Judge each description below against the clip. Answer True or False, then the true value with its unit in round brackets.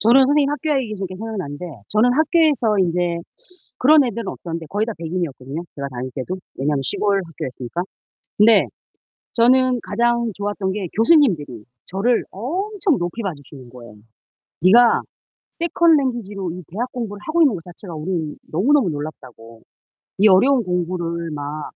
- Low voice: False (195 Hz)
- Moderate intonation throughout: False (6.6 semitones)